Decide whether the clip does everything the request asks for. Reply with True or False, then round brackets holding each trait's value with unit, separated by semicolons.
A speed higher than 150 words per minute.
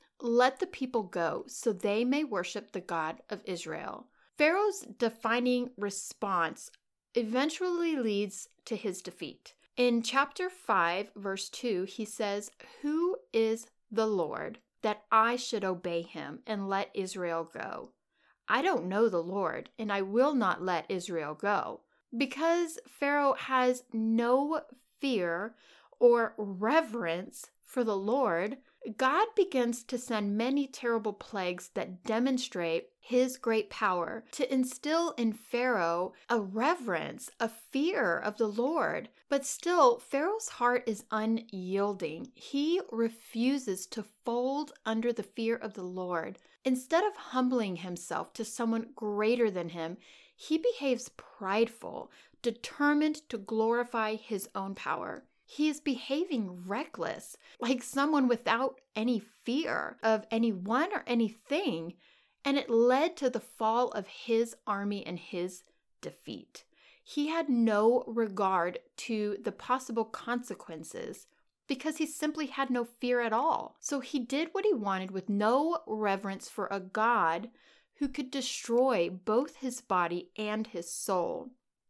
False (135 wpm)